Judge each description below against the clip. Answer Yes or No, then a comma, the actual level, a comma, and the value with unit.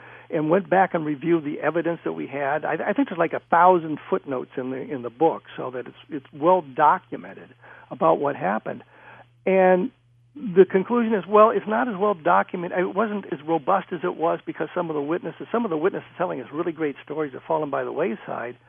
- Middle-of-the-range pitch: Yes, medium, 170 Hz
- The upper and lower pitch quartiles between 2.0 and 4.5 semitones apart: Yes, average, 4.0 semitones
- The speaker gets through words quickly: Yes, fast, 220 wpm